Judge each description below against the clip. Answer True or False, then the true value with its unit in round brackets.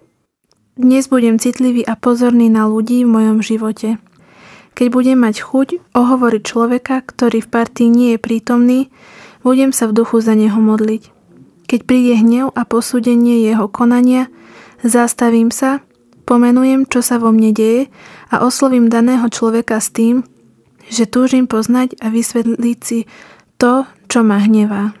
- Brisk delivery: False (145 wpm)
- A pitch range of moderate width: False (1.9 semitones)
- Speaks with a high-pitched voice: True (235 Hz)